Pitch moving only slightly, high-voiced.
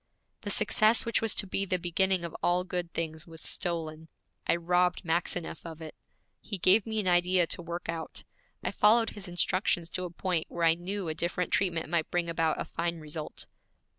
No: narrow, 2.1 semitones; medium, 175 Hz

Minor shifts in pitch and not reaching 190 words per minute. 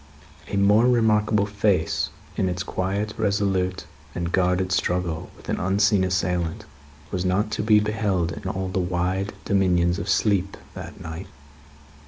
Yes: narrow, 2.3 semitones; average, 145 wpm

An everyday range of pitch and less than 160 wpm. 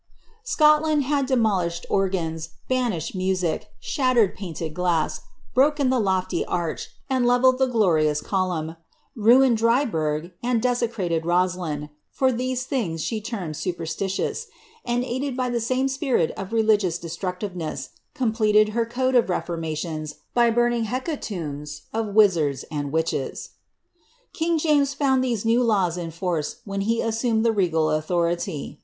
No: wide, 6.8 semitones; average, 140 wpm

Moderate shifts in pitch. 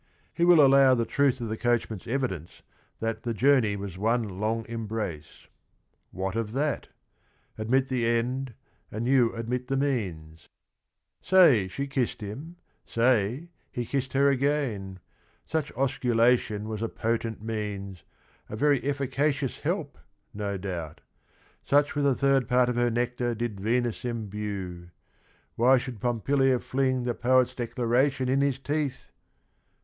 Yes: average, 3.8 semitones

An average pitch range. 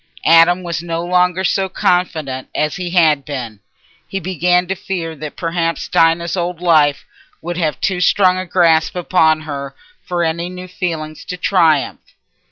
No: narrow, 2.3 semitones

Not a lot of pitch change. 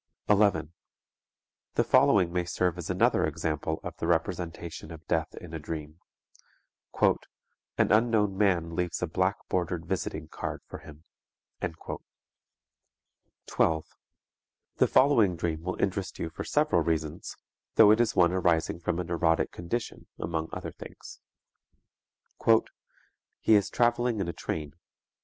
No: average, 3.3 semitones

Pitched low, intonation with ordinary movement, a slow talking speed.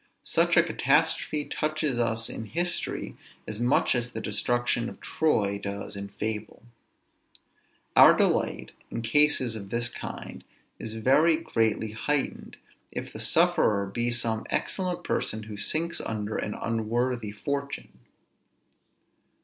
Yes: low, 115 Hz; average, 4.5 semitones; slow, 125 wpm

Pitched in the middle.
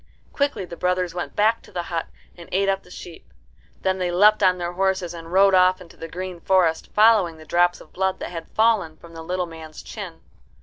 Yes: medium, 180 Hz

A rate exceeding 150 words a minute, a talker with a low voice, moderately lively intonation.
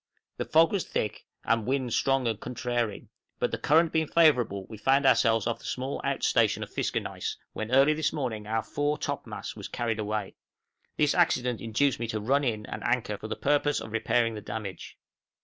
Yes: average, 195 wpm; low, 120 Hz; average, 4.4 semitones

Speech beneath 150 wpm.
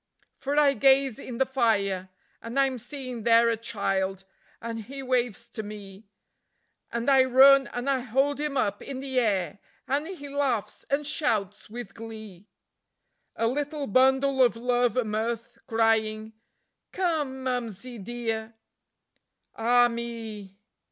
Yes: average, 140 wpm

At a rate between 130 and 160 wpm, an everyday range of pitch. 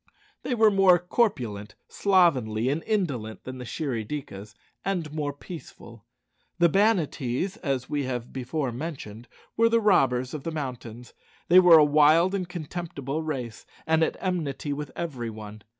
No: average, 150 wpm; wide, 6.1 semitones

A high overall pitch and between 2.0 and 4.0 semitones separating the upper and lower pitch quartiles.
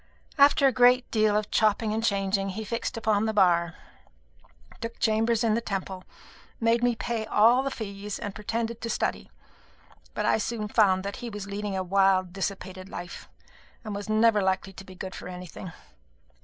Yes: high, 210 Hz; average, 2.9 semitones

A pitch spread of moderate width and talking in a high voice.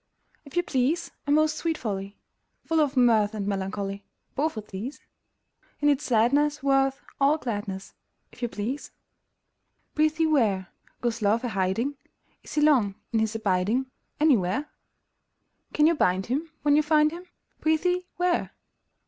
No: wide, 6.4 semitones; very high, 265 Hz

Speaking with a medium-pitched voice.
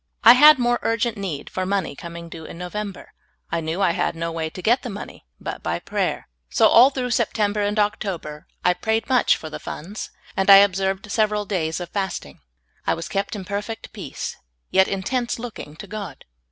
No: high, 200 Hz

